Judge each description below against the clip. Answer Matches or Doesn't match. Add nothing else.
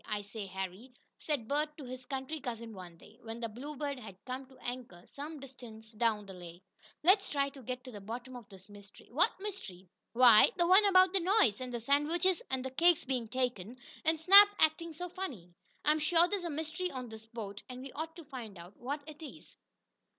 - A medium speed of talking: Doesn't match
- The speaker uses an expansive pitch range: Matches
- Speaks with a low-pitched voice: Doesn't match